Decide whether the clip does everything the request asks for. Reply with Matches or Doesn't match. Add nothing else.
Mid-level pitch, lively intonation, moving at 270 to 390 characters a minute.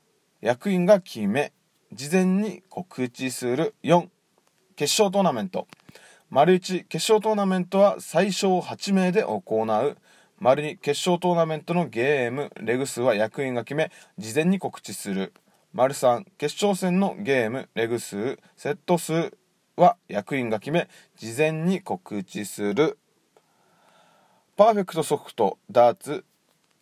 Doesn't match